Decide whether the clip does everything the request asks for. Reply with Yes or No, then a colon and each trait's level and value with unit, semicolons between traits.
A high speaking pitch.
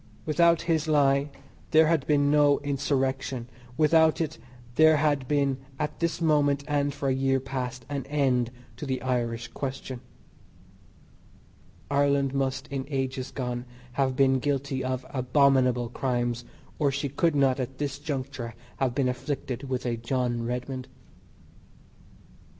No: low, 135 Hz